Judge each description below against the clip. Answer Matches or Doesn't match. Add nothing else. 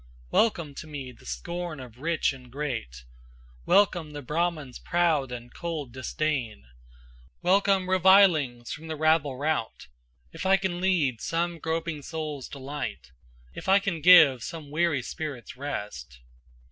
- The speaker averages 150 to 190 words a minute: Doesn't match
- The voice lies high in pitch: Doesn't match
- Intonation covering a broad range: Doesn't match